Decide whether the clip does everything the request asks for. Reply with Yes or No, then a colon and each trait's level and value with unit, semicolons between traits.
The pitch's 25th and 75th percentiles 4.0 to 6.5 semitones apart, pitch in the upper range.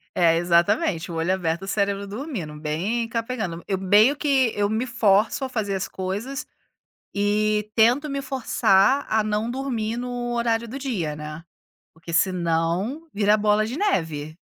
Yes: average, 5.2 semitones; high, 210 Hz